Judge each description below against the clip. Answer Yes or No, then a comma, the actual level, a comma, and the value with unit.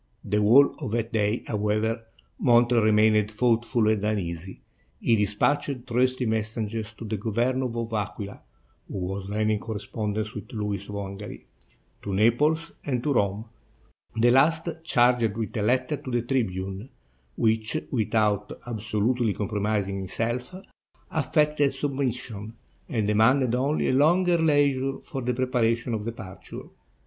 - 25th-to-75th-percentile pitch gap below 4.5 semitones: Yes, average, 3.4 semitones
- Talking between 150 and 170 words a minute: No, average, 140 wpm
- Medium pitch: No, low, 115 Hz